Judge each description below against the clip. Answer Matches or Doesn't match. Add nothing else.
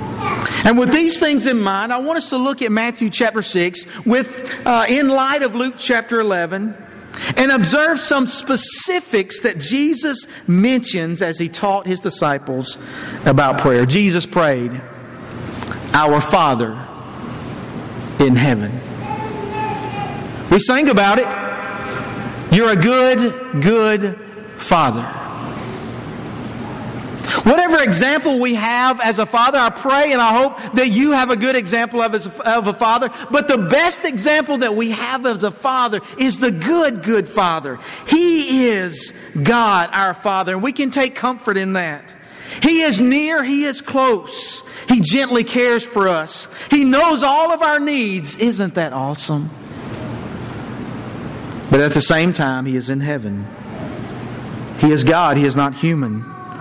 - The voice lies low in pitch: Doesn't match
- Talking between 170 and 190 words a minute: Doesn't match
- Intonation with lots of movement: Matches